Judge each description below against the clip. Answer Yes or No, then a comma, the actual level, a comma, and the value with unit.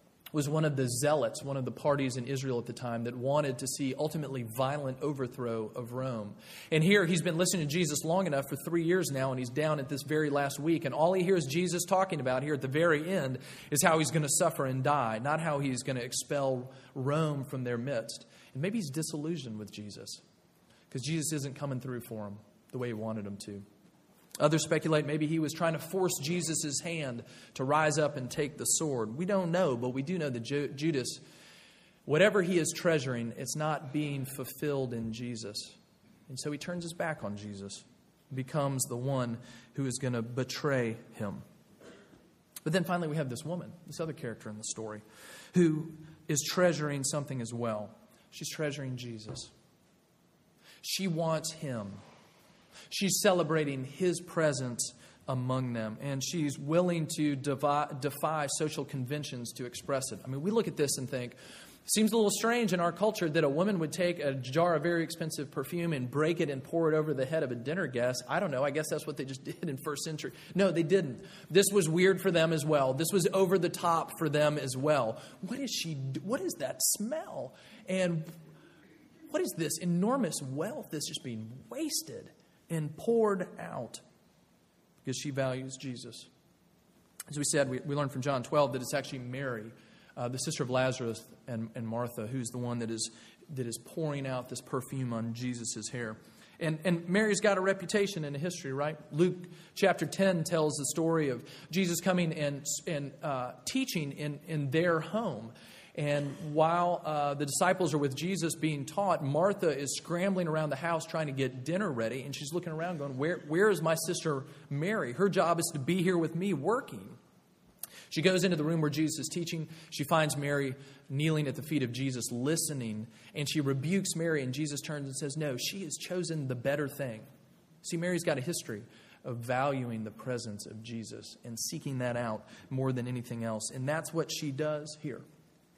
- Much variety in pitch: No, average, 4.4 semitones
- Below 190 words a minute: No, average, 200 wpm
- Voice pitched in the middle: Yes, medium, 150 Hz